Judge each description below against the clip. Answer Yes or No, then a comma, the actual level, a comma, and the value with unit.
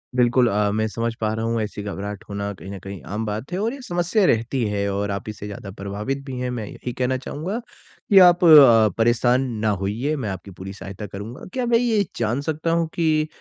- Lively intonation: Yes, wide, 6.8 semitones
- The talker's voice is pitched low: Yes, low, 115 Hz